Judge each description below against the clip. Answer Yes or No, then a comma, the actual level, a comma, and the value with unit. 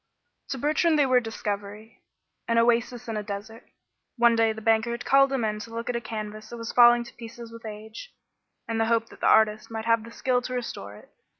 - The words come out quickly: Yes, fast, 230 wpm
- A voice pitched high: Yes, high, 230 Hz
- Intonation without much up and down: Yes, narrow, 1.5 semitones